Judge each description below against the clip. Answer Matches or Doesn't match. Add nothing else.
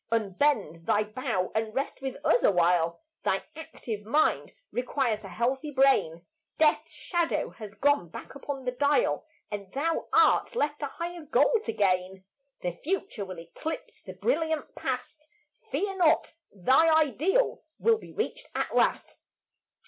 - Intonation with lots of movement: Matches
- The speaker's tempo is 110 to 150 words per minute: Matches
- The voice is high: Matches